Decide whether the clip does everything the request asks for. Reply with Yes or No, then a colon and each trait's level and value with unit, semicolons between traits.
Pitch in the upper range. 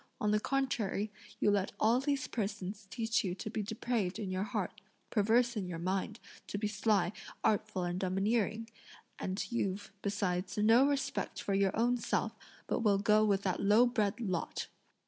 Yes: high, 210 Hz